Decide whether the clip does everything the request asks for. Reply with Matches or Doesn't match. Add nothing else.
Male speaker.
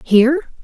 Doesn't match